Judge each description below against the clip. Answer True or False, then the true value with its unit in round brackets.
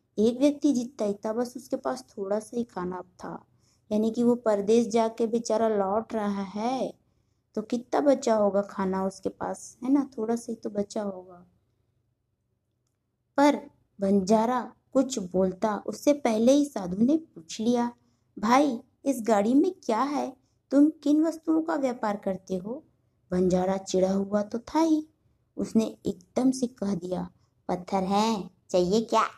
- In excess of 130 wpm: True (155 wpm)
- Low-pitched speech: False (220 Hz)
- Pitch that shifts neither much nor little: True (4.6 semitones)